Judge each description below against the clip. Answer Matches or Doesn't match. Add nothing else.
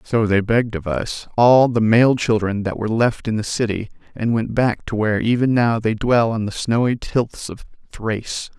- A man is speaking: Matches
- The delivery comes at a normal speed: Doesn't match